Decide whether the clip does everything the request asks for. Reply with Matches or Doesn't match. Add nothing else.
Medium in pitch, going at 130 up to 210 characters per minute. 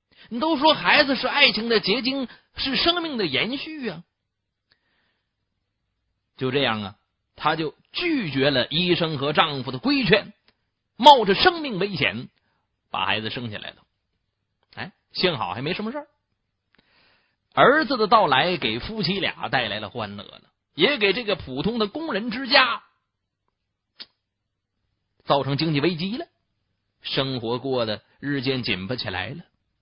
Matches